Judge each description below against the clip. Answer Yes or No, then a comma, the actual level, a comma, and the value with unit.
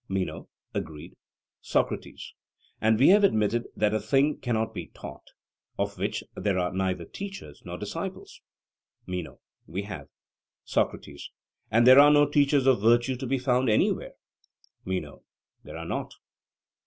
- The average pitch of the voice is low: Yes, low, 115 Hz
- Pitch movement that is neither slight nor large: No, wide, 6.0 semitones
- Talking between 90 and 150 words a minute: Yes, average, 140 wpm